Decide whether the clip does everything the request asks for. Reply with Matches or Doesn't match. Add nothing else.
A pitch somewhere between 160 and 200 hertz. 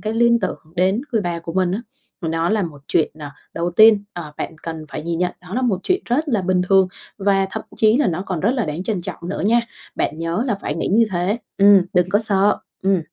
Matches